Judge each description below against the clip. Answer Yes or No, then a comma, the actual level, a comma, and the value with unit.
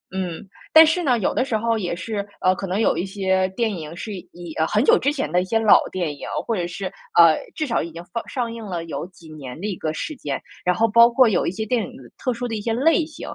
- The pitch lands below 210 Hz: Yes, high, 200 Hz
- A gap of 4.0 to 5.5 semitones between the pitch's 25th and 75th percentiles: Yes, average, 5.0 semitones